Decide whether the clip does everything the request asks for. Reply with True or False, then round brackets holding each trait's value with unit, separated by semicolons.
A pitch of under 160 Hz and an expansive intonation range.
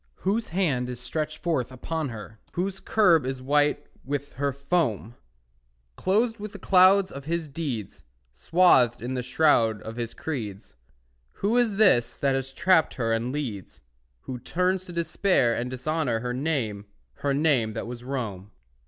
True (140 Hz; 5.9 semitones)